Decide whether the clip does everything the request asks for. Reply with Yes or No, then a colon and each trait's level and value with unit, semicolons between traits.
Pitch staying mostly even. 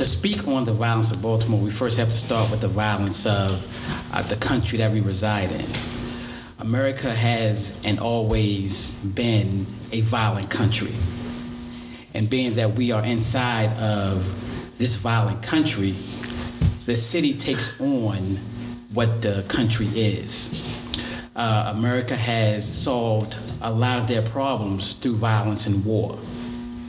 Yes: narrow, 2.2 semitones